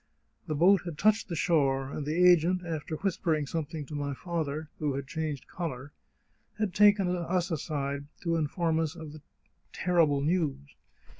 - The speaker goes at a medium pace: Yes, average, 165 wpm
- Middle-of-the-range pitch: Yes, medium, 160 Hz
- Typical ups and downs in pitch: Yes, average, 3.4 semitones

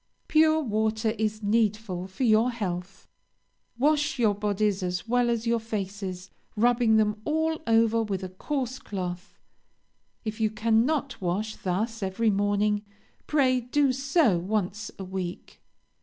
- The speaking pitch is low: No, high, 215 Hz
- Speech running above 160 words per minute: No, slow, 135 wpm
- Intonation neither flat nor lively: Yes, average, 3.6 semitones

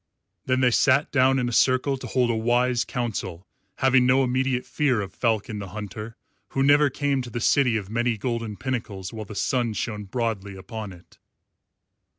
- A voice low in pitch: Yes, low, 120 Hz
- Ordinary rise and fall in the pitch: Yes, average, 3.3 semitones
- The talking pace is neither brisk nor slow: Yes, average, 180 wpm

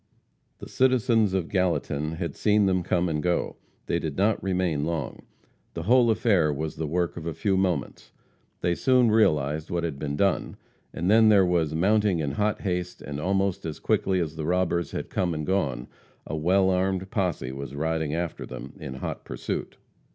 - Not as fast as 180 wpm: No, average, 185 wpm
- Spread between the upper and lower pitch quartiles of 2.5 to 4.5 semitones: Yes, average, 3.7 semitones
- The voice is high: No, very low, 90 Hz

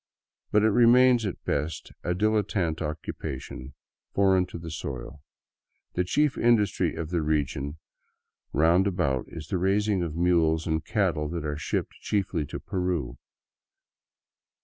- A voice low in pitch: Yes, very low, 85 Hz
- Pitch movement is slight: No, average, 4.4 semitones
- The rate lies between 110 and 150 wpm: Yes, slow, 135 wpm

